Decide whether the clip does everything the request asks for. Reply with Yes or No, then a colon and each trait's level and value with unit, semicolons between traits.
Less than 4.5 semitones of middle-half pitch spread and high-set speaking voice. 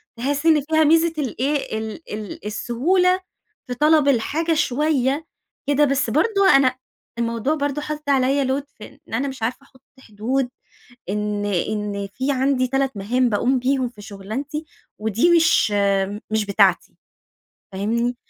No: average, 5.0 semitones; very high, 265 Hz